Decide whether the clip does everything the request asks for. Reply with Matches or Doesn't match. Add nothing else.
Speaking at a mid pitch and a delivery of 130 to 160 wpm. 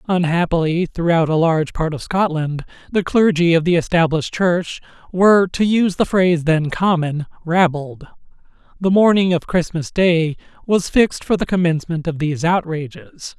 Matches